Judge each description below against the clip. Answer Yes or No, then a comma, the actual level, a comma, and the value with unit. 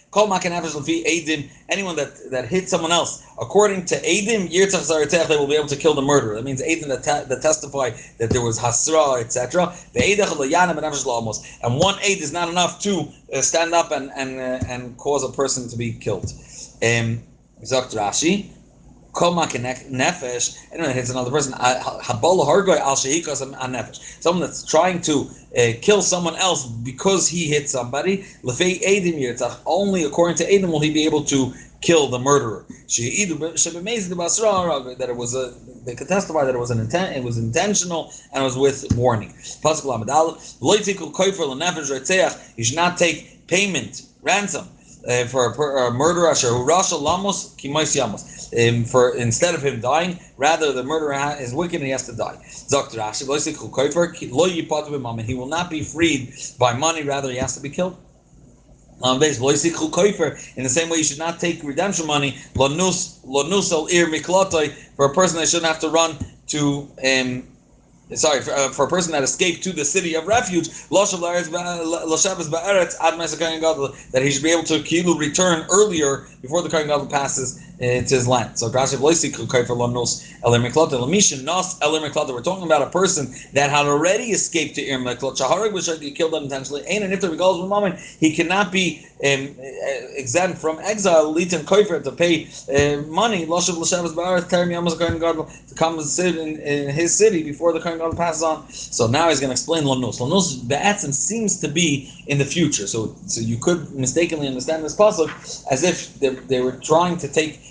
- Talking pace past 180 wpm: No, average, 165 wpm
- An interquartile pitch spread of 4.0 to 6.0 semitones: Yes, average, 4.5 semitones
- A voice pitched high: No, medium, 155 Hz